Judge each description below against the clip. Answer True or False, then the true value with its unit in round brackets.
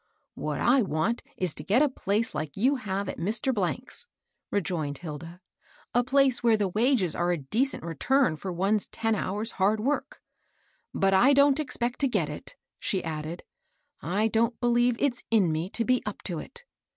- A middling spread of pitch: False (5.9 semitones)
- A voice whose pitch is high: True (215 Hz)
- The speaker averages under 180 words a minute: False (190 wpm)